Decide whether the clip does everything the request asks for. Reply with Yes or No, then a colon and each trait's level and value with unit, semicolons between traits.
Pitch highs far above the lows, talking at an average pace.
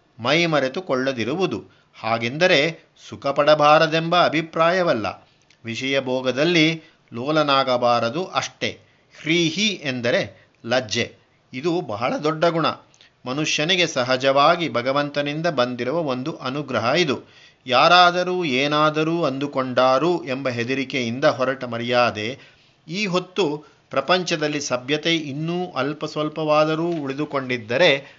No: average, 4.1 semitones; average, 80 wpm